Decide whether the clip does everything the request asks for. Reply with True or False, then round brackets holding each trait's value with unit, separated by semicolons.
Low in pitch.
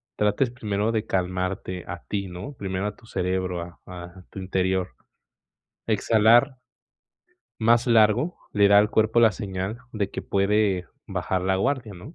True (100 Hz)